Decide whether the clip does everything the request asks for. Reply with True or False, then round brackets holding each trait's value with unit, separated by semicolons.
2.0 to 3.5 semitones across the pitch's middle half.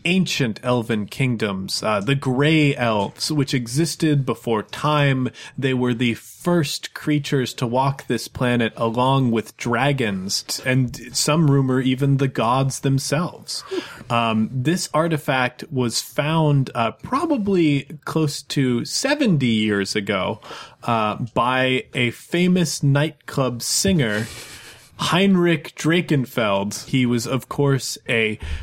False (4.2 semitones)